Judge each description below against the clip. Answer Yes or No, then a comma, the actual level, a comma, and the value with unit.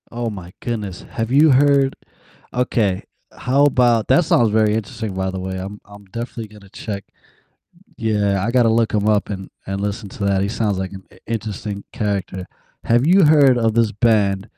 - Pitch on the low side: Yes, low, 110 Hz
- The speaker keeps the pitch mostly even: No, average, 3.2 semitones